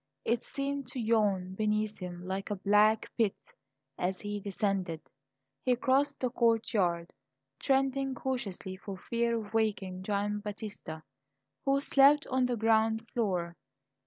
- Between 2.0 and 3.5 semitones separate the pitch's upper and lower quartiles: No, average, 4.0 semitones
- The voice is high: Yes, high, 215 Hz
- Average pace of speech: No, slow, 130 wpm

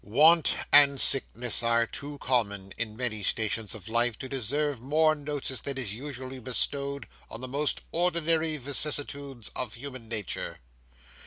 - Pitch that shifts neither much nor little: Yes, average, 3.8 semitones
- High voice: No, low, 130 Hz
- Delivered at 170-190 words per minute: No, average, 145 wpm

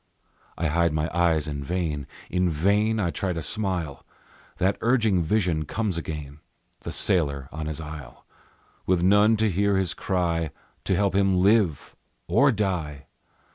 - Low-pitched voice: Yes, very low, 90 Hz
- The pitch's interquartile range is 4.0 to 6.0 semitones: Yes, average, 4.4 semitones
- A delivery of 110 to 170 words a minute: Yes, average, 150 wpm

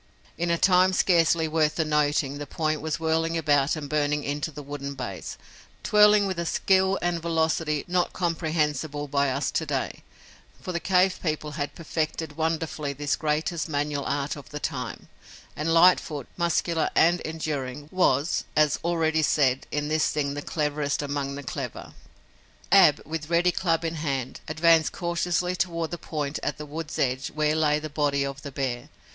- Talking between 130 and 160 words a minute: No, average, 170 wpm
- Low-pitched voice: No, medium, 155 Hz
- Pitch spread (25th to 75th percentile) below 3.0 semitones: Yes, narrow, 2.5 semitones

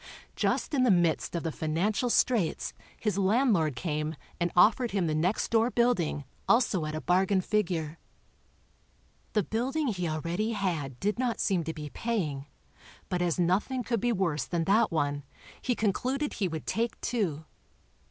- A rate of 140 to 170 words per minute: Yes, average, 160 wpm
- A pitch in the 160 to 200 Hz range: Yes, medium, 185 Hz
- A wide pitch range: Yes, wide, 6.0 semitones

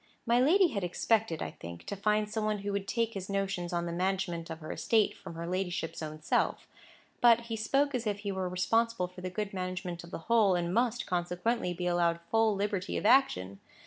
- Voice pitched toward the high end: Yes, high, 195 Hz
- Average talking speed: No, fast, 215 wpm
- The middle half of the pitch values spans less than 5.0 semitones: Yes, average, 4.0 semitones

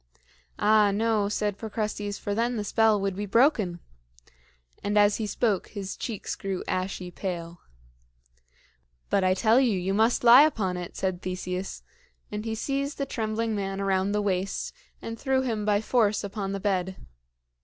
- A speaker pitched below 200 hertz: No, high, 205 Hz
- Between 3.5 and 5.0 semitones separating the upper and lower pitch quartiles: No, narrow, 2.5 semitones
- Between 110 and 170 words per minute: Yes, average, 165 wpm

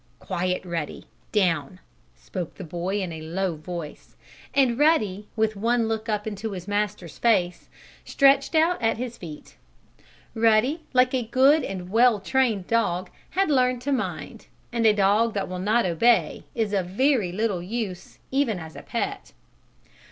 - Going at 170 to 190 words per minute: No, average, 160 wpm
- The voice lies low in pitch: No, high, 210 Hz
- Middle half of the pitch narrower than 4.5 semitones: No, average, 5.0 semitones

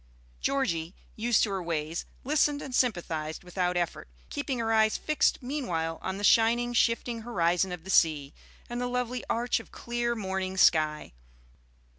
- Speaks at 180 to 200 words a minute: No, average, 155 wpm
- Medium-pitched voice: No, high, 215 Hz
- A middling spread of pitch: No, wide, 5.9 semitones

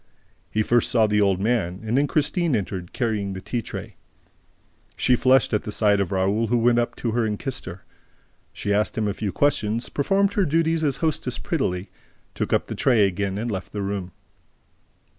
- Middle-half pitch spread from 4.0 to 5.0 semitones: Yes, average, 4.6 semitones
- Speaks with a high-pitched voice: No, low, 110 Hz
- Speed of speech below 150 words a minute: No, average, 200 wpm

